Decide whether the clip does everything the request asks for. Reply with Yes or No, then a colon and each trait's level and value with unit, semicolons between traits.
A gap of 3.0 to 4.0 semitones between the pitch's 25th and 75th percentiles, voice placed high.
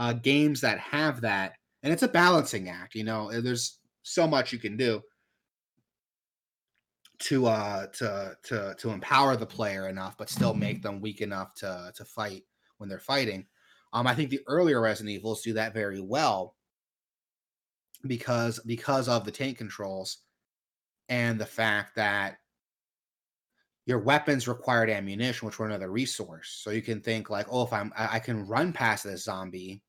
No: average, 3.3 semitones; low, 110 Hz